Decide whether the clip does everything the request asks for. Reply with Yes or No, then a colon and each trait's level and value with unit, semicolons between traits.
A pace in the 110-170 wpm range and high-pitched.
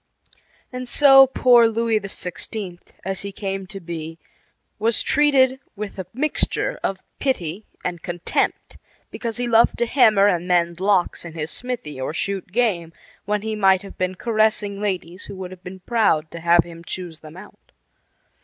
Yes: average, 165 wpm; high, 195 Hz